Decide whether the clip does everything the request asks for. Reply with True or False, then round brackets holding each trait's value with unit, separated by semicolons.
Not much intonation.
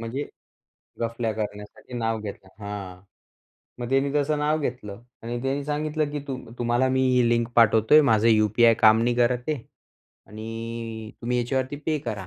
False (3.2 semitones)